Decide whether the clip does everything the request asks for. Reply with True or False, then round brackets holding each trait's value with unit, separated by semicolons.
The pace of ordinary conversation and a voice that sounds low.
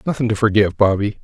True (195 wpm; 105 Hz)